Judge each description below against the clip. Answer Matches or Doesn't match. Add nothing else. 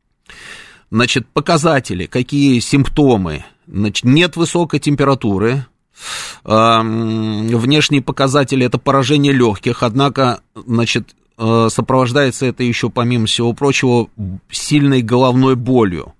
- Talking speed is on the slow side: Matches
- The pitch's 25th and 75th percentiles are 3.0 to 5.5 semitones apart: Matches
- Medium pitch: Doesn't match